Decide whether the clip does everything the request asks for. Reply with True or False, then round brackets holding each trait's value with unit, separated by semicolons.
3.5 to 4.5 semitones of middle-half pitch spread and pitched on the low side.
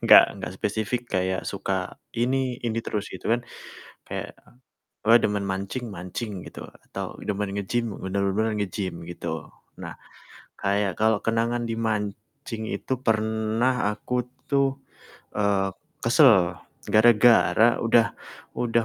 False (3.0 semitones; 110 Hz)